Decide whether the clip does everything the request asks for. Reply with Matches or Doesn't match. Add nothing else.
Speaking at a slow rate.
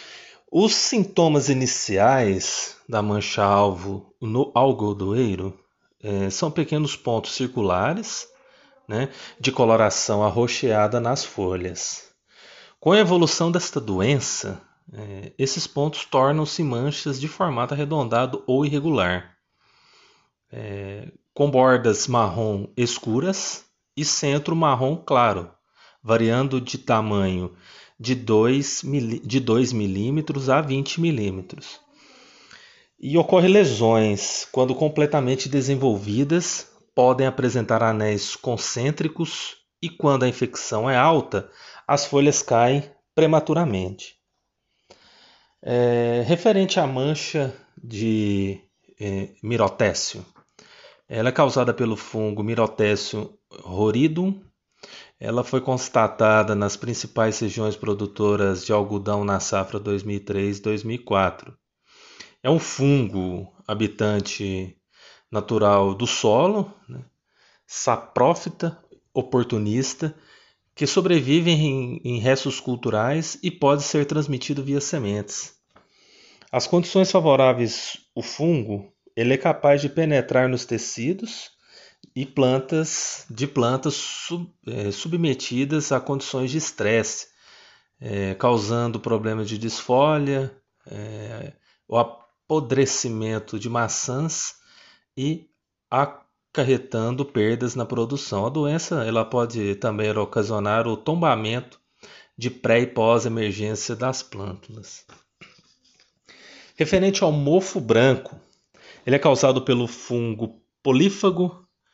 Matches